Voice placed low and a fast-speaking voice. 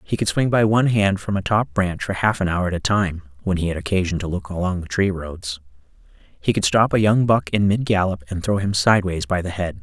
Yes: very low, 95 Hz; fast, 265 wpm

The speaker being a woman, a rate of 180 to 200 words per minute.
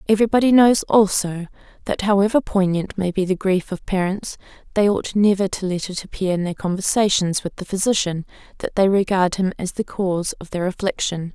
Yes: female; average, 190 wpm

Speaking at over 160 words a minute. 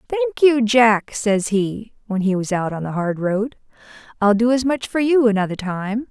Yes: fast, 205 wpm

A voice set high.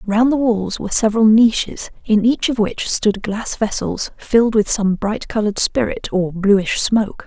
Yes: high, 215 Hz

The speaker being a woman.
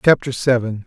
No: male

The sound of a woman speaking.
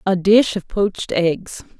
Yes: female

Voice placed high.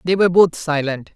No: medium, 165 Hz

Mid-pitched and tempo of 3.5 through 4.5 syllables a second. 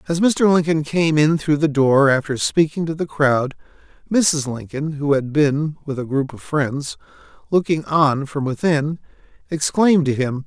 Yes: medium, 150 Hz; 4.4 syllables/s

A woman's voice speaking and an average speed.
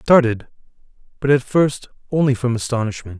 No: male; average, 150 wpm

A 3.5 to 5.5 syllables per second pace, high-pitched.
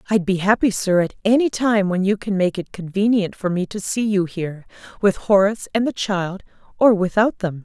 Yes: 5.3 syllables/s; high, 195 Hz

